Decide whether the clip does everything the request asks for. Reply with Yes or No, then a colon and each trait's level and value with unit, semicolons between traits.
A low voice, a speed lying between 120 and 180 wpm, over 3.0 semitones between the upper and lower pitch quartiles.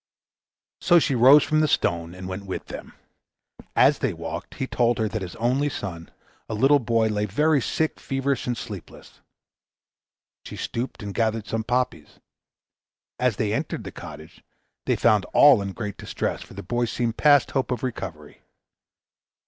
Yes: low, 115 Hz; average, 165 wpm; average, 4.8 semitones